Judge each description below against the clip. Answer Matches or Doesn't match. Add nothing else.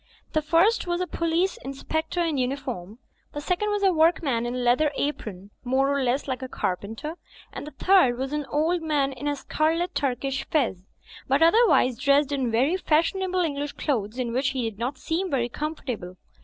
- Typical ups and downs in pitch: Matches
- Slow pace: Doesn't match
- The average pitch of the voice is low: Doesn't match